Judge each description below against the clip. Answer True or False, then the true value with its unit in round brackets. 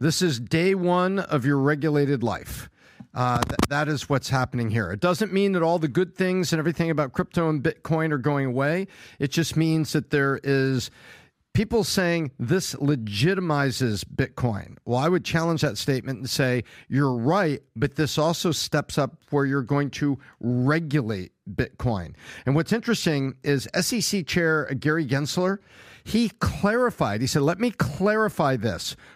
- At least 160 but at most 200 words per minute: True (165 wpm)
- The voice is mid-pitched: True (150 Hz)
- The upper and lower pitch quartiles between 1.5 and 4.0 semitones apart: False (4.5 semitones)